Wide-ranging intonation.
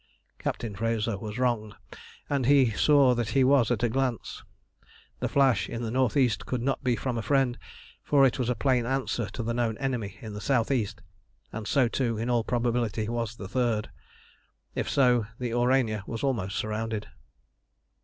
No: narrow, 2.6 semitones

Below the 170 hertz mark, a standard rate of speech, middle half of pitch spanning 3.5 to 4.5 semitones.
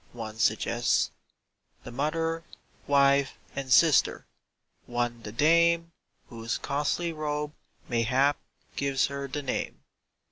No: medium, 140 Hz; slow, 105 wpm; average, 4.0 semitones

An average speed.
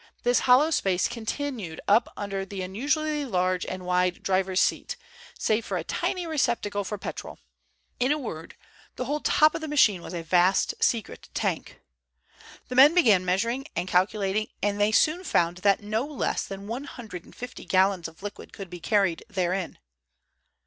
Yes: average, 175 wpm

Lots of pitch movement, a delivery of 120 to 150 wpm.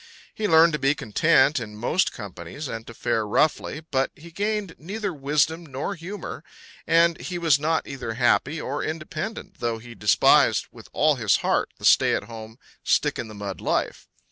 No: wide, 6.2 semitones; average, 180 wpm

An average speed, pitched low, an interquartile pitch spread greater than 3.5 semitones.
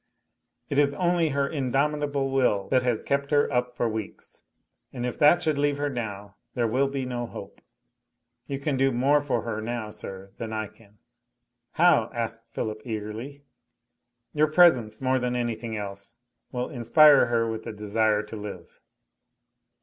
Yes: average, 165 wpm; low, 125 Hz; average, 4.2 semitones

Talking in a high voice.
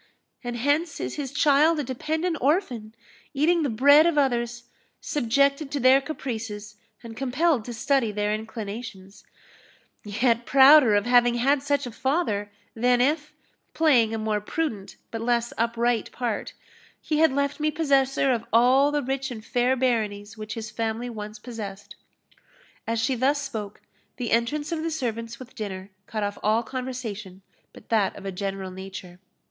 Yes: high, 240 Hz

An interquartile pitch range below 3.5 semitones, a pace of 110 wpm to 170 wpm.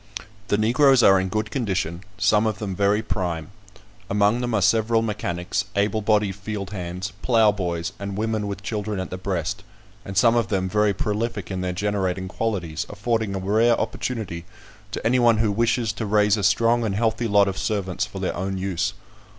No: average, 2.8 semitones; average, 185 wpm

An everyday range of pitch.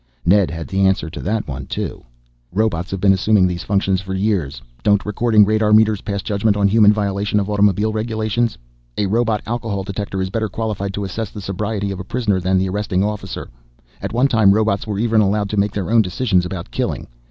No: narrow, 2.2 semitones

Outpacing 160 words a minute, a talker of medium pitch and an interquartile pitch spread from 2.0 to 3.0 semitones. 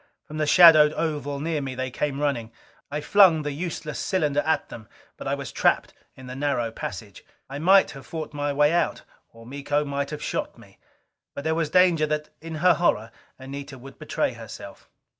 Yes: average, 195 wpm; medium, 145 Hz; narrow, 2.6 semitones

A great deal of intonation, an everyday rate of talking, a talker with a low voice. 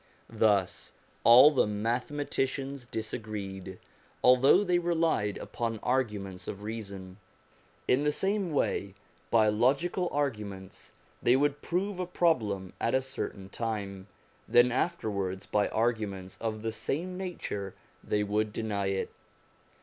No: wide, 5.8 semitones; slow, 125 wpm; low, 115 Hz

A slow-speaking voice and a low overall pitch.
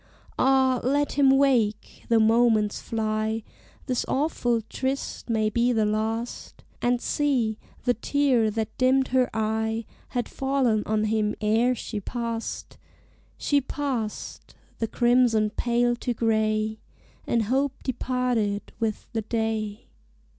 No: slow, 125 wpm; high, 230 Hz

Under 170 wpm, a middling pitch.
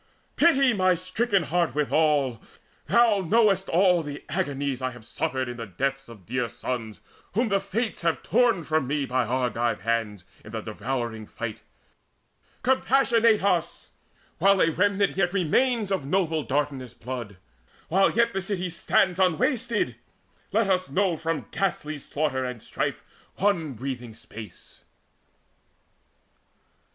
Yes: slow, 135 wpm; medium, 160 Hz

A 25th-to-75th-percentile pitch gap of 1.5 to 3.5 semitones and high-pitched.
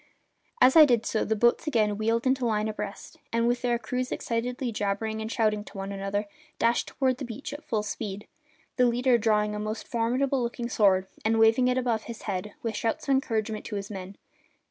Yes: average, 2.7 semitones; high, 225 Hz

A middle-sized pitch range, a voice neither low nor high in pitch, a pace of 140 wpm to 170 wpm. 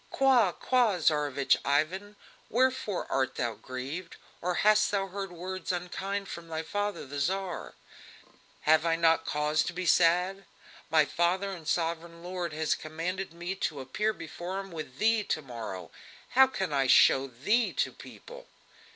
Yes: average, 4.1 semitones; medium, 175 Hz; average, 155 wpm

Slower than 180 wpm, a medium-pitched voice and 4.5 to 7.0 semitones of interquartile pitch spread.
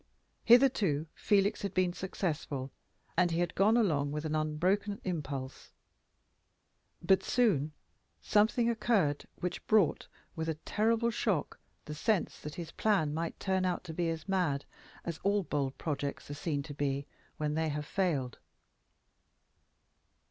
Yes: average, 140 wpm; medium, 170 Hz; average, 5.1 semitones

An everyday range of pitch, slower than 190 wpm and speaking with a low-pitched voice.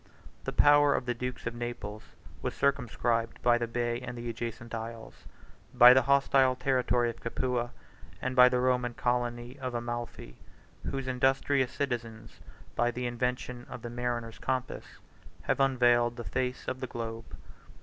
No: narrow, 1.3 semitones; average, 160 wpm; low, 120 Hz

